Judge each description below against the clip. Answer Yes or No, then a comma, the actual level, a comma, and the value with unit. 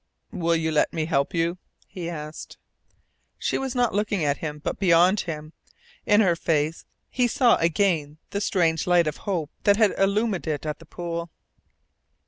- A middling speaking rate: Yes, average, 170 wpm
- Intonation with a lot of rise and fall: No, average, 4.2 semitones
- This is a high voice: No, medium, 170 Hz